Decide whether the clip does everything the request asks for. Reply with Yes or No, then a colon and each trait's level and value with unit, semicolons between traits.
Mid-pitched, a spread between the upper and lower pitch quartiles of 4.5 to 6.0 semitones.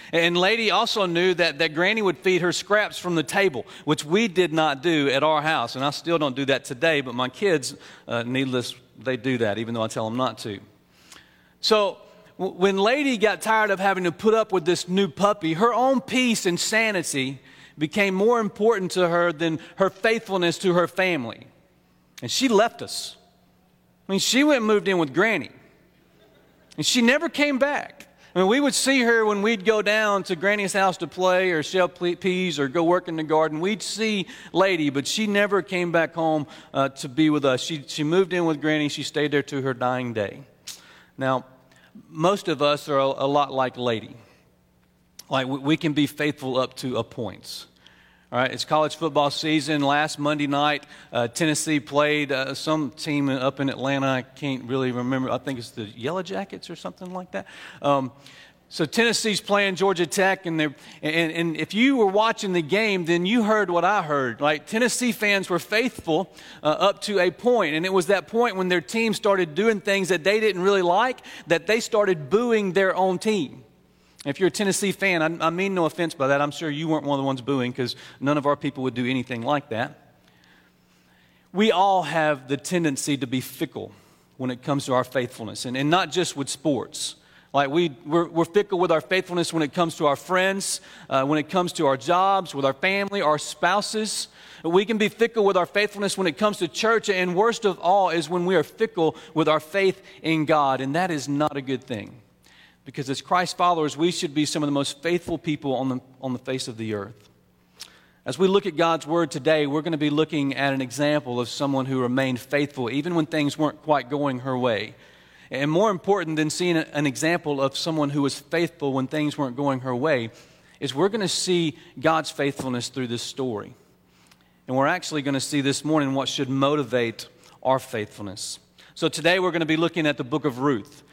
Yes: medium, 155 Hz; wide, 5.5 semitones